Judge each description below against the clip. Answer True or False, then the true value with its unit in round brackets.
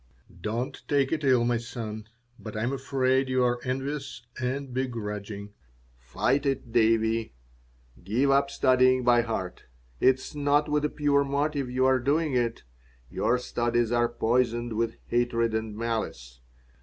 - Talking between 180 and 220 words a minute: False (150 wpm)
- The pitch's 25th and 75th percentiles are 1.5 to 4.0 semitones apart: True (2.9 semitones)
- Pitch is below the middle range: True (120 Hz)